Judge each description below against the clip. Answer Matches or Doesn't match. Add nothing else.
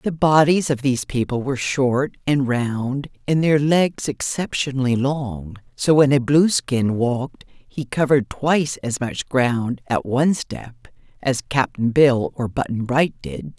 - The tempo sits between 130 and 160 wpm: Matches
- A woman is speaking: Matches